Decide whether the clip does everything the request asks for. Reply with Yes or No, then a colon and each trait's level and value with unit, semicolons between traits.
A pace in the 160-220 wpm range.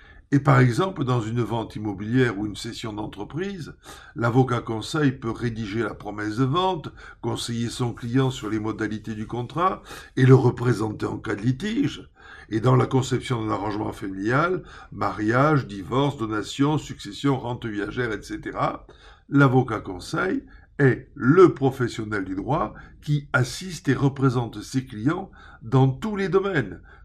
No: slow, 145 wpm